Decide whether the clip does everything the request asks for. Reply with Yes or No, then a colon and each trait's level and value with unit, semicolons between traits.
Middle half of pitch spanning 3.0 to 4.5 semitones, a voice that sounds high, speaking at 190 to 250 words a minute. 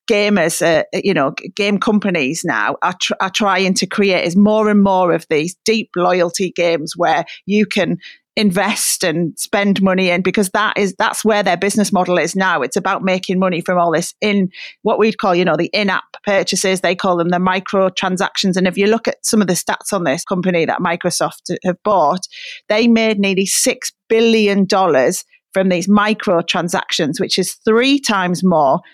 No: narrow, 2.6 semitones; high, 195 Hz; average, 195 wpm